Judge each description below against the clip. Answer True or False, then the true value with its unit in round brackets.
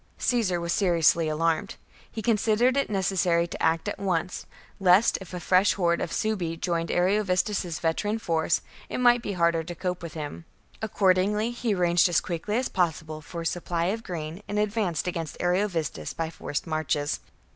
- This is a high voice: False (180 Hz)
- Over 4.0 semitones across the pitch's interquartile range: False (3.7 semitones)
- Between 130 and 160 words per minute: False (170 wpm)